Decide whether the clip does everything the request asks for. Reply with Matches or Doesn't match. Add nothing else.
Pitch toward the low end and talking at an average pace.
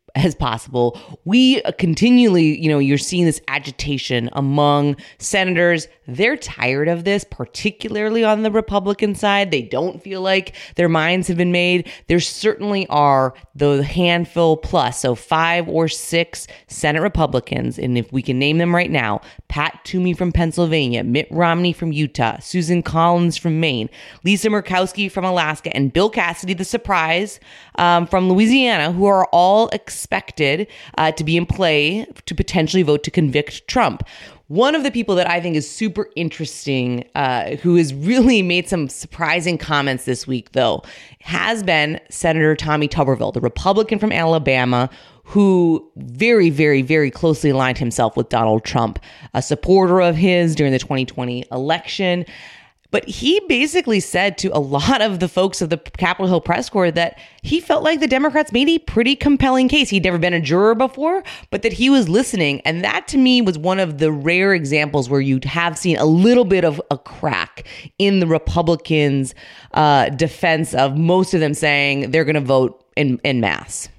Doesn't match